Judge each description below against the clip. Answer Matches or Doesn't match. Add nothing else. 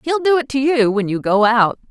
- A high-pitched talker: Matches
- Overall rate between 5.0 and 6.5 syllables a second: Matches